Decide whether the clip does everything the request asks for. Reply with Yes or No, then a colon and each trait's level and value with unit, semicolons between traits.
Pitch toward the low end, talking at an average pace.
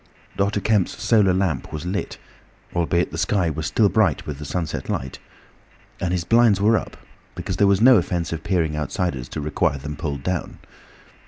Yes: very low, 90 Hz; average, 180 wpm